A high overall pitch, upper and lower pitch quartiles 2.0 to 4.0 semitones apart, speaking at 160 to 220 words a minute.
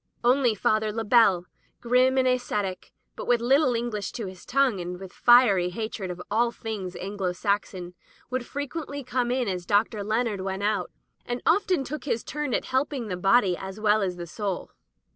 No: high, 220 Hz; average, 4.6 semitones; average, 180 wpm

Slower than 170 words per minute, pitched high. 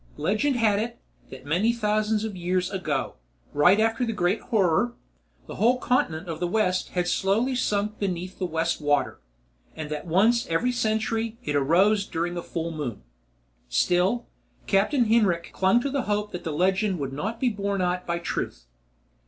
No: average, 175 wpm; high, 195 Hz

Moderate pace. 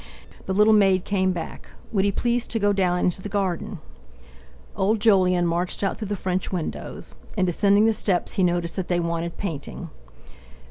Yes: average, 180 wpm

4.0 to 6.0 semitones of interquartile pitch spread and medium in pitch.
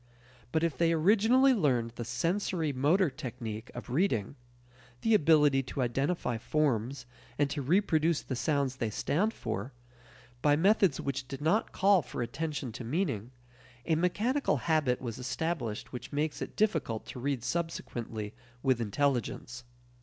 Yes: average, 5.3 semitones; medium, 145 Hz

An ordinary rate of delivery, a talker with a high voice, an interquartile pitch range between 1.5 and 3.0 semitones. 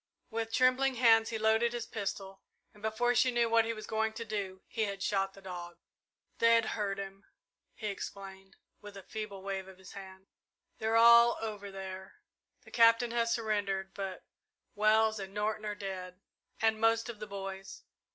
Yes: average, 175 wpm; high, 210 Hz; average, 2.7 semitones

